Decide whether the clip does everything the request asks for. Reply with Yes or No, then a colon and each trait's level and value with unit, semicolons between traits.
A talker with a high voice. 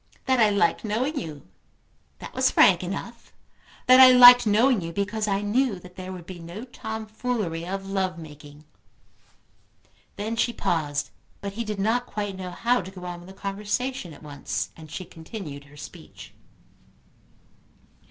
Yes: high, 195 Hz